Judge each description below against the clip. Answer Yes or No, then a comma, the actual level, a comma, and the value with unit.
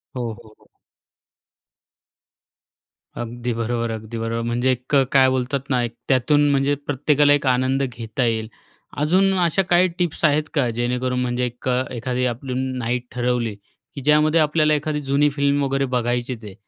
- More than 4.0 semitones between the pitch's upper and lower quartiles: No, average, 3.2 semitones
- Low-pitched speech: Yes, low, 130 Hz